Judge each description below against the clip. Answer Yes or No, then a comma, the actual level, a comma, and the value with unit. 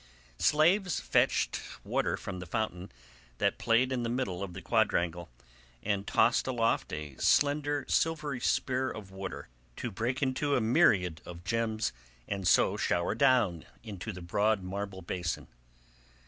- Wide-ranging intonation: Yes, wide, 5.9 semitones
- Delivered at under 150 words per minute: Yes, average, 140 wpm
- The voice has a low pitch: Yes, low, 110 Hz